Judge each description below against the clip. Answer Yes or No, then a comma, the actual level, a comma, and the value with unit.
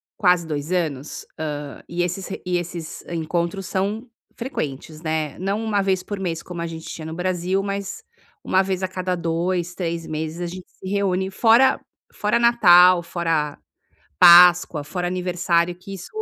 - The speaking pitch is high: No, medium, 180 Hz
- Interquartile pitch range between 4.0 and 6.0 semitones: No, narrow, 2.4 semitones